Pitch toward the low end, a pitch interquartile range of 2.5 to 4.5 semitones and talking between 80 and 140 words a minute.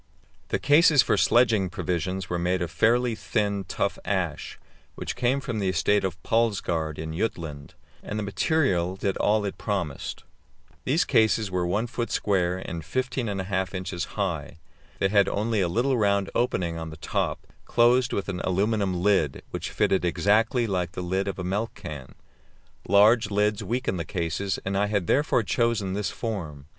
No: low, 100 Hz; average, 3.9 semitones; average, 170 wpm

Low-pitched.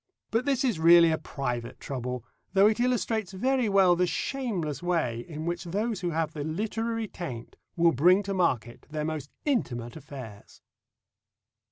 No: medium, 170 Hz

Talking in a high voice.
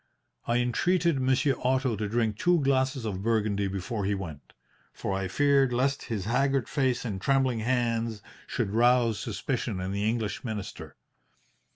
No: low, 115 Hz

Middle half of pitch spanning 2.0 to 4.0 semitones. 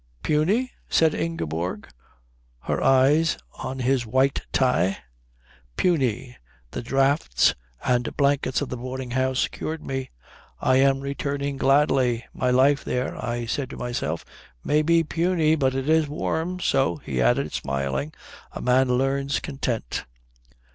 Yes: average, 2.8 semitones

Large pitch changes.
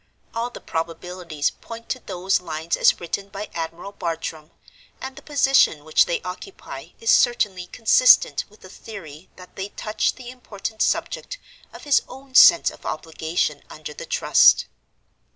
Yes: wide, 6.2 semitones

